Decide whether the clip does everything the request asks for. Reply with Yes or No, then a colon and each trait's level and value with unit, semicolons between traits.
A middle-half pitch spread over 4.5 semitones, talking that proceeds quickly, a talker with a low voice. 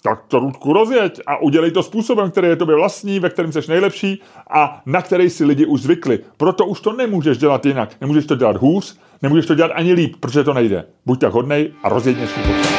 No: average, 5.2 semitones; fast, 220 wpm; medium, 165 Hz